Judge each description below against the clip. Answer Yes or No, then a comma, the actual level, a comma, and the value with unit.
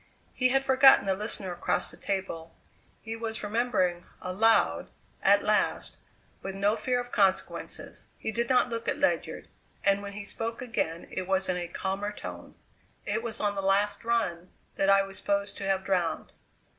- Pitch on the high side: Yes, high, 200 Hz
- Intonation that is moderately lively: Yes, average, 3.1 semitones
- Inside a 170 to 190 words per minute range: Yes, average, 175 wpm